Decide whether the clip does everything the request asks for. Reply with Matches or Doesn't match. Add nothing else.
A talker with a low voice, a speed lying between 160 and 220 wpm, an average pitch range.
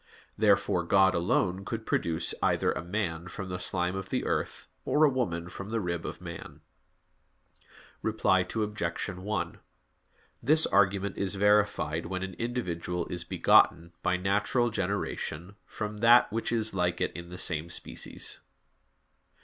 Doesn't match